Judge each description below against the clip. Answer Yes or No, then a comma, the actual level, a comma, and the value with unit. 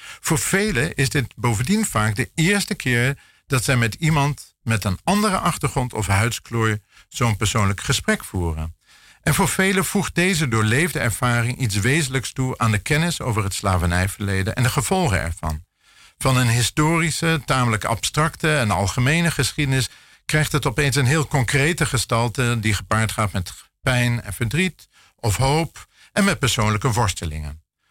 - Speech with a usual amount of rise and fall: No, wide, 5.8 semitones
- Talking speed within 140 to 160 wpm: Yes, average, 155 wpm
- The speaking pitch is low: Yes, low, 125 Hz